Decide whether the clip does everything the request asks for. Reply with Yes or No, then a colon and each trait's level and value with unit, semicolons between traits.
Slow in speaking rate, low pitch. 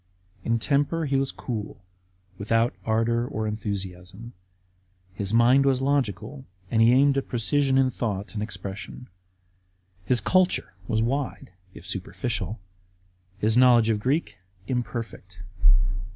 Yes: slow, 125 wpm; low, 115 Hz